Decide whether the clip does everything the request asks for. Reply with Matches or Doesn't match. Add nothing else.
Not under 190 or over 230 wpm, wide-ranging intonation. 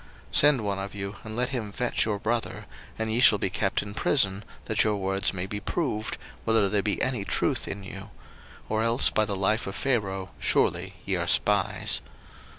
Doesn't match